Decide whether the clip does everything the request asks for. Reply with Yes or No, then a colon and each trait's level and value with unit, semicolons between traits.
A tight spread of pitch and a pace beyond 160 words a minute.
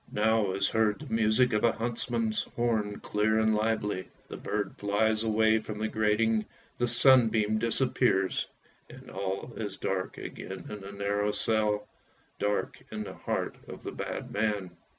No: narrow, 1.5 semitones; average, 155 wpm